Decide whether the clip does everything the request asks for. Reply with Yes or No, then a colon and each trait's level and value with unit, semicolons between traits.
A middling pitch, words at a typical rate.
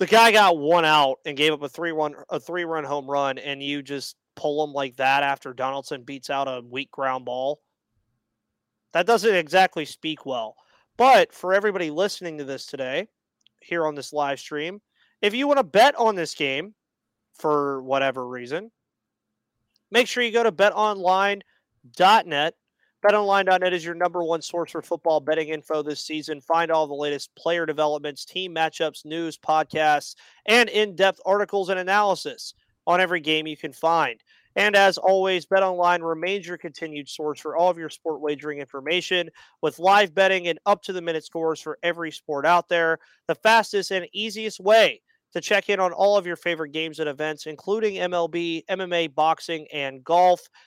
Yes: medium, 165 Hz; average, 175 wpm